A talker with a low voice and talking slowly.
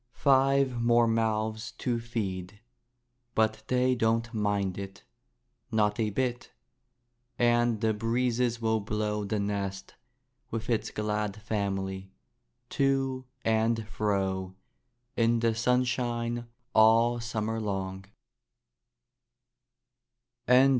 Yes: low, 110 Hz; slow, 95 wpm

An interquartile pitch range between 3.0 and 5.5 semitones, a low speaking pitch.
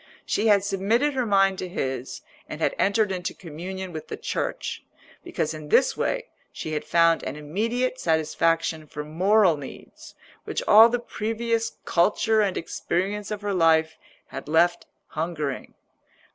No: average, 5.0 semitones; medium, 185 Hz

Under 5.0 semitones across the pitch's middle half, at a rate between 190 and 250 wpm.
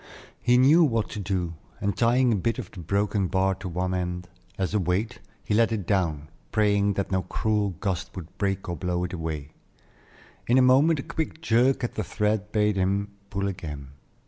Yes: average, 3.6 semitones; average, 200 wpm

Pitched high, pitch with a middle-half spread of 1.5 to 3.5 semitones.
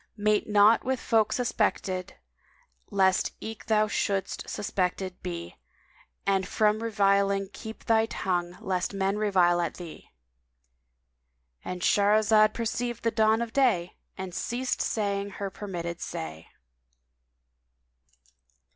Yes: high, 200 Hz; average, 2.9 semitones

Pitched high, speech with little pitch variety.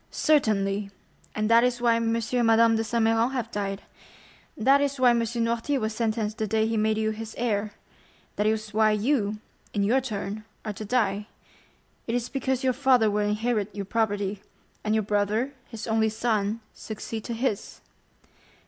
Yes: high, 220 Hz; narrow, 2.1 semitones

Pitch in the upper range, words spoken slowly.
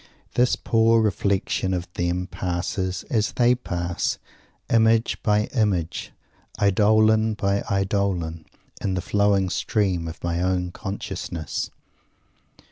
No: low, 100 Hz; slow, 110 wpm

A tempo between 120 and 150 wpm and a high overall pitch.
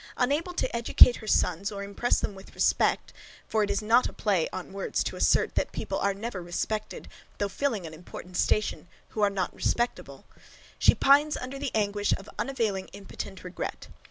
No: average, 185 wpm; high, 205 Hz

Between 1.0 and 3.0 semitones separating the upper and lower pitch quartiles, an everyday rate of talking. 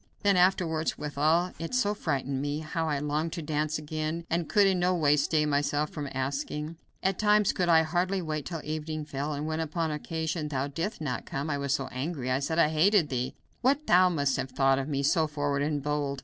No: average, 2.7 semitones; fast, 220 wpm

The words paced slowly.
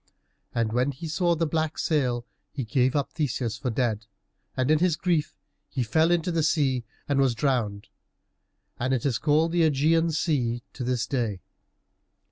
No: average, 170 wpm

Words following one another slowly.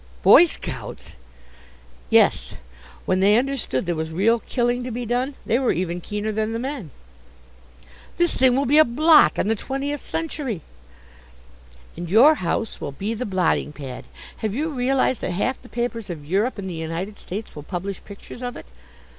No: average, 175 wpm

